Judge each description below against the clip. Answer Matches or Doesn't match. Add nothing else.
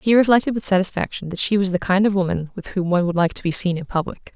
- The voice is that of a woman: Matches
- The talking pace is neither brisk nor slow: Doesn't match